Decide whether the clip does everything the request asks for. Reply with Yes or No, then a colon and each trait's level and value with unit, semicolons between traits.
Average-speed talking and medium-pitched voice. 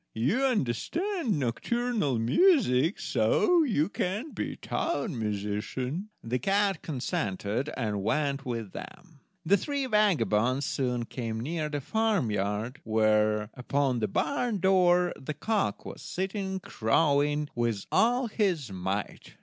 No: slow, 120 wpm; medium, 145 Hz